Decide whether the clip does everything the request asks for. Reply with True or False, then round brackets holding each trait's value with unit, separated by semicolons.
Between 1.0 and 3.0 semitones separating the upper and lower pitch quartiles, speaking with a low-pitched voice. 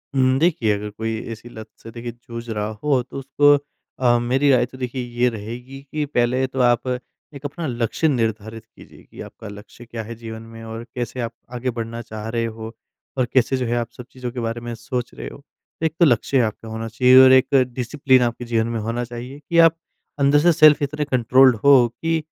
True (2.7 semitones; 120 Hz)